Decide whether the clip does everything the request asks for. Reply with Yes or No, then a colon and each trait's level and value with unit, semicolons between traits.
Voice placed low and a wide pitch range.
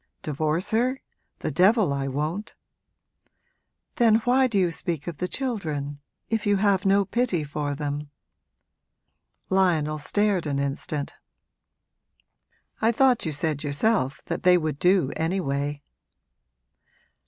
No: medium, 175 Hz; wide, 6.0 semitones